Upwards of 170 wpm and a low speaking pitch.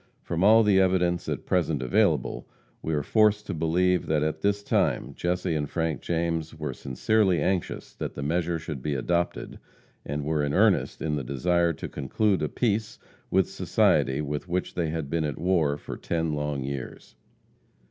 Yes: average, 180 wpm; very low, 80 Hz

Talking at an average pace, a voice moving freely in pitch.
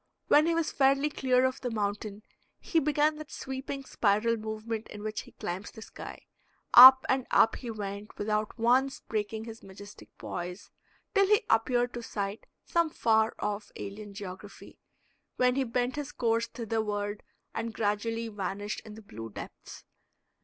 No: average, 160 wpm; average, 3.9 semitones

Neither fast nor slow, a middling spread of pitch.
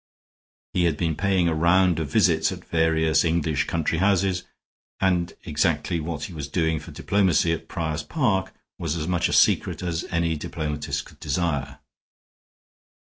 No: average, 155 wpm; narrow, 2.3 semitones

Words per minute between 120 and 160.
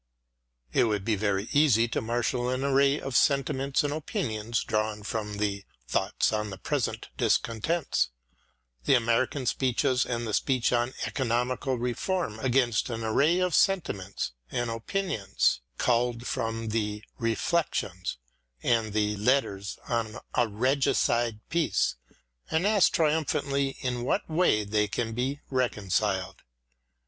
Yes: average, 140 wpm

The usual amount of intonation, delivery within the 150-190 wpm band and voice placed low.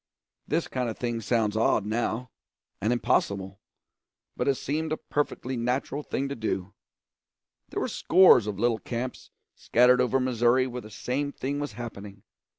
Yes: average, 3.1 semitones; average, 155 wpm; low, 120 Hz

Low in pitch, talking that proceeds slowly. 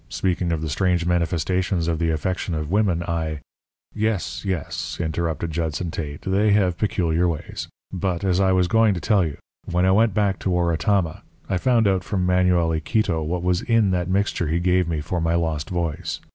No: very low, 90 Hz; average, 195 wpm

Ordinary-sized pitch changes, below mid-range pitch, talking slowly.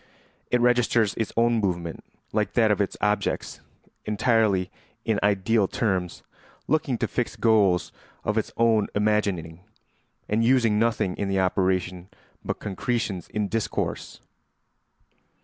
Yes: average, 3.4 semitones; low, 105 Hz; slow, 125 wpm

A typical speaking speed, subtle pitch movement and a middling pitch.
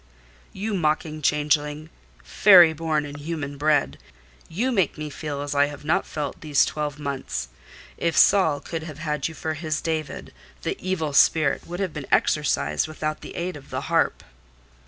Yes: average, 165 wpm; narrow, 2.0 semitones; medium, 155 Hz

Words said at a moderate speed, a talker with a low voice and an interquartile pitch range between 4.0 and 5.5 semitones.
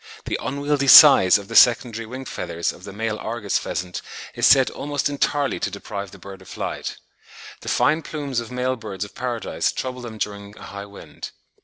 Yes: average, 190 wpm; low, 115 Hz; average, 4.7 semitones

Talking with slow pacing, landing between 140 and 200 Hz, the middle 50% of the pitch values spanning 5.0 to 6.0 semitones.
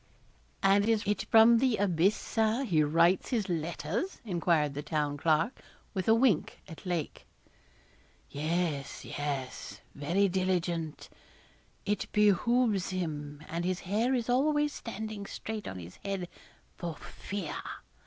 Yes: slow, 130 wpm; medium, 185 Hz; wide, 5.4 semitones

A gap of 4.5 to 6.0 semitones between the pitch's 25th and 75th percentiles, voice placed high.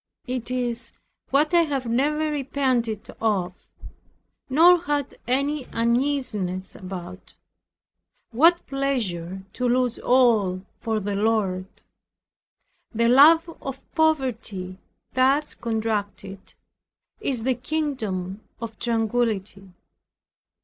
Yes: average, 5.1 semitones; high, 235 Hz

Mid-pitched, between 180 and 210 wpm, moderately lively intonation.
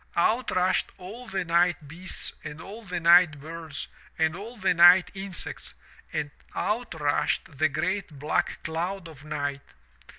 No: medium, 170 Hz; average, 145 wpm; average, 3.4 semitones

